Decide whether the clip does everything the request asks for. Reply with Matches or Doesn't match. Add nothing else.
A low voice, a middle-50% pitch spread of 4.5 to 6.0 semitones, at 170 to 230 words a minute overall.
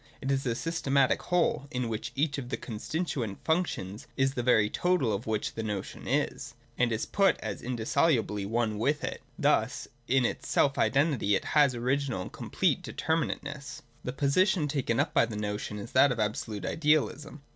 Matches